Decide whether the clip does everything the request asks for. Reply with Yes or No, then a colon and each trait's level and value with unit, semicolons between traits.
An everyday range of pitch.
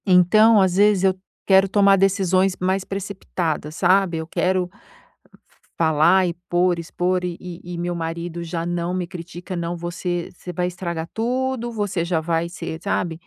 No: narrow, 2.1 semitones